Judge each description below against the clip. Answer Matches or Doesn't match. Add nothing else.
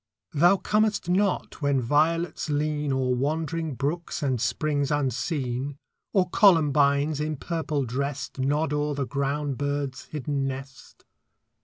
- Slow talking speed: Matches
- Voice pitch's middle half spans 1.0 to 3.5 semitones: Matches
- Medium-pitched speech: Matches